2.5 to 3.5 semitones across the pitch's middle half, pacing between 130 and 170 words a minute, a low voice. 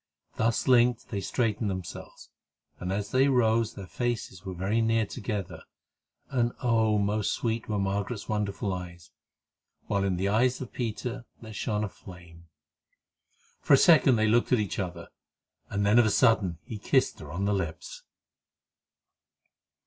Yes: average, 3.2 semitones; average, 155 wpm; low, 105 Hz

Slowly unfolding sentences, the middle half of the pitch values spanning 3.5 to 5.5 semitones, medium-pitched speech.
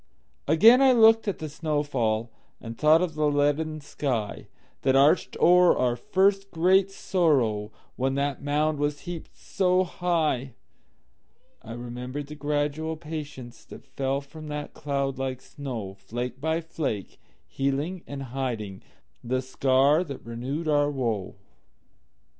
Yes: slow, 120 wpm; average, 3.8 semitones; medium, 145 Hz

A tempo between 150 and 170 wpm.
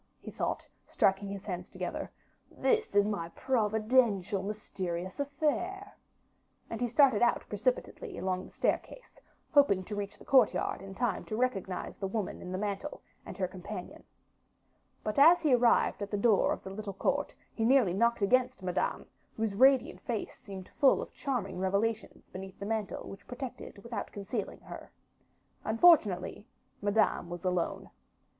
Yes: average, 155 wpm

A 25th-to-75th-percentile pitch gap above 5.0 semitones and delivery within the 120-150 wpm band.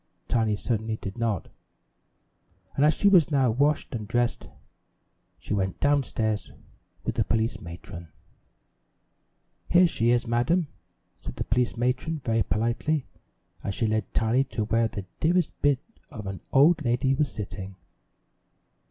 No: average, 4.7 semitones; average, 145 wpm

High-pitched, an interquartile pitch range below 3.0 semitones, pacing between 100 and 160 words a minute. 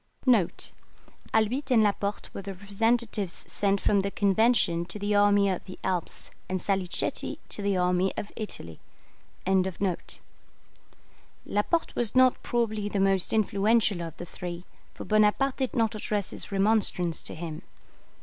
Yes: high, 200 Hz; narrow, 2.6 semitones; average, 140 wpm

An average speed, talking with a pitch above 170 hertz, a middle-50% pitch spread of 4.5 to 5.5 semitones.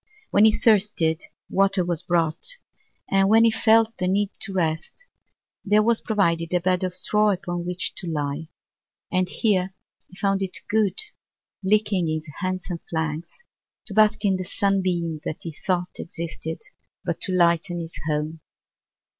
No: average, 155 wpm; medium, 185 Hz; average, 3.3 semitones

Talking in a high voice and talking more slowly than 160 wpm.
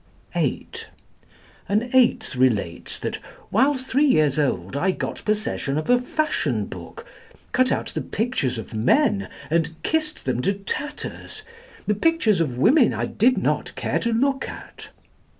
Yes: high, 215 Hz; average, 150 wpm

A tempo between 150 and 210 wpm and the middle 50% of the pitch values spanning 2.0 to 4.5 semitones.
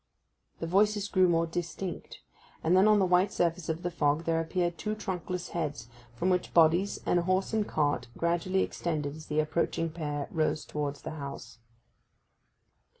Yes: average, 170 wpm; average, 3.0 semitones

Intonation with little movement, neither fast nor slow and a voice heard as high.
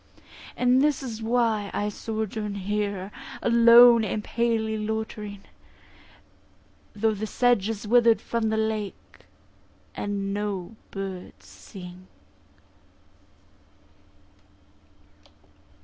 No: narrow, 2.2 semitones; slow, 85 wpm; high, 220 Hz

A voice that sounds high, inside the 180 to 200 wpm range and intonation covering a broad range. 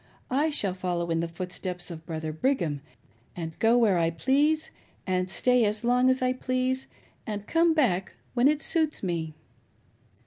No: high, 205 Hz; average, 165 wpm; wide, 7.1 semitones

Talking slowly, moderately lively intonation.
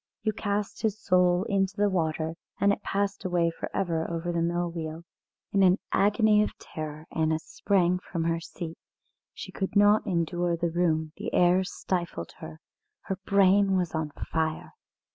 No: average, 165 wpm; average, 3.1 semitones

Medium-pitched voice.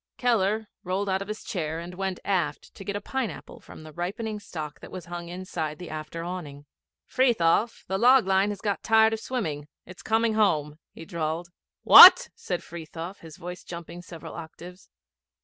Yes: medium, 180 Hz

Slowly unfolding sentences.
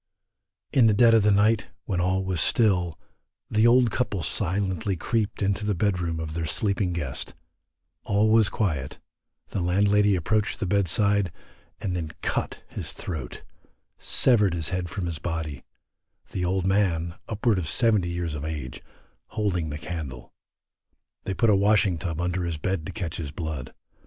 No: average, 165 wpm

